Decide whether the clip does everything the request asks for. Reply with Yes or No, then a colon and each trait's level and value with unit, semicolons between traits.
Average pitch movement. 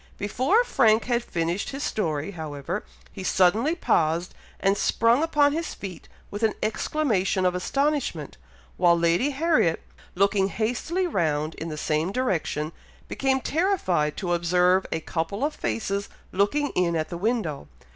No: wide, 7.5 semitones